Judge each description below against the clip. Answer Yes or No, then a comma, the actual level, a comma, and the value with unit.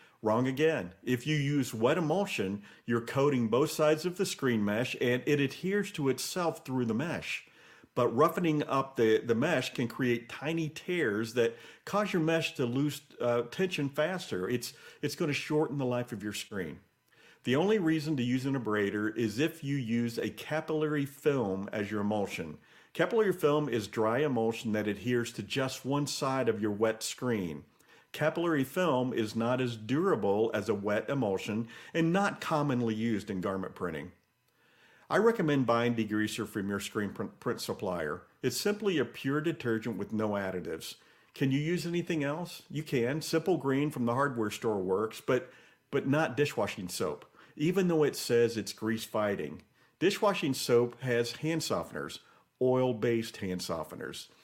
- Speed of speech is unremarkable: Yes, average, 170 wpm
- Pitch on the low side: Yes, low, 130 Hz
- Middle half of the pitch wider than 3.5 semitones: Yes, average, 5.2 semitones